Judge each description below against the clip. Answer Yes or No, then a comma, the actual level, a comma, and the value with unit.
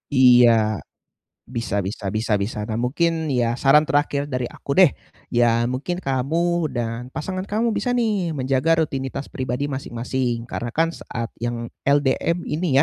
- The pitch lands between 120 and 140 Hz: Yes, low, 135 Hz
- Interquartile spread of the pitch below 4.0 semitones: No, average, 5.3 semitones